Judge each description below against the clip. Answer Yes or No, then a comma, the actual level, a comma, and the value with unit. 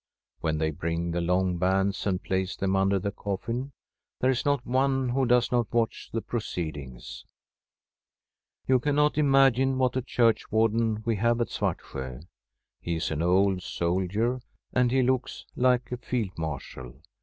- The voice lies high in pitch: No, low, 110 Hz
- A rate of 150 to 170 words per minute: Yes, average, 155 wpm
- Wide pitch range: Yes, wide, 5.8 semitones